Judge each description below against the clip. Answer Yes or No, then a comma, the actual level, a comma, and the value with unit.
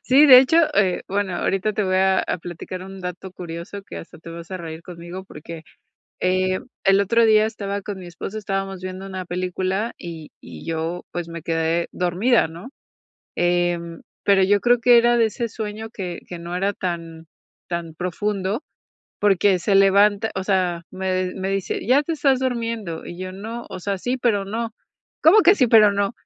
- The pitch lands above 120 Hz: Yes, high, 190 Hz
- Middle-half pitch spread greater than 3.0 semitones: Yes, average, 3.4 semitones